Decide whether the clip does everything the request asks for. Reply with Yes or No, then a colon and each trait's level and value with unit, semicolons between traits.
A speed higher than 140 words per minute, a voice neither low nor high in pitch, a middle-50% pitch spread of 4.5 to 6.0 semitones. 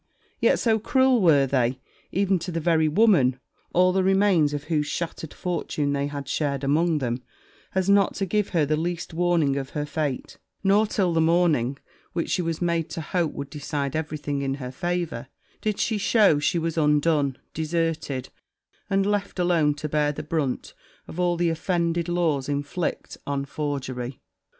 No: average, 175 wpm; medium, 160 Hz; average, 3.7 semitones